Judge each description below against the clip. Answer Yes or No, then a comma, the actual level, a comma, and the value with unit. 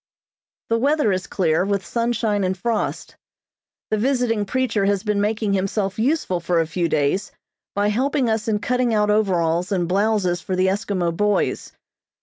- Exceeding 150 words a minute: Yes, average, 160 wpm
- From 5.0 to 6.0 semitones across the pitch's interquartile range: No, average, 3.4 semitones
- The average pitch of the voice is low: No, high, 205 Hz